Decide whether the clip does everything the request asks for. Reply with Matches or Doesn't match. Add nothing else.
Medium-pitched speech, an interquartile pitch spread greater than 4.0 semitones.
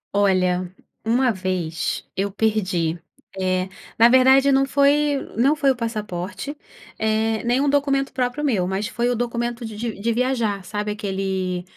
Doesn't match